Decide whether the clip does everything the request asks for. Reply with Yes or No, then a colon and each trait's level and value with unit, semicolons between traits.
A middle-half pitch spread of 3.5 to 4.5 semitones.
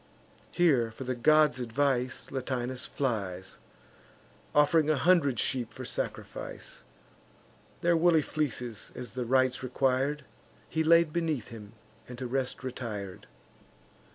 Yes: average, 3.8 semitones